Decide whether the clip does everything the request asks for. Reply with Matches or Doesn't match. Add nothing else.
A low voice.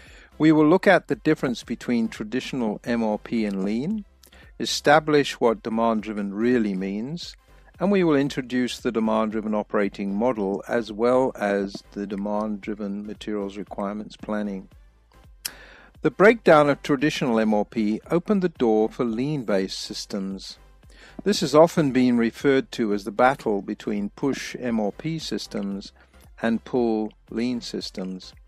Matches